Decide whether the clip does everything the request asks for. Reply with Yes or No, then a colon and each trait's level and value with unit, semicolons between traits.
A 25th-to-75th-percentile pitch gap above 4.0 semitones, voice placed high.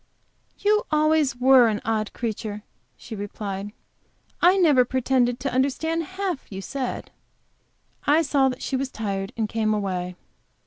Yes: wide, 5.4 semitones; very high, 250 Hz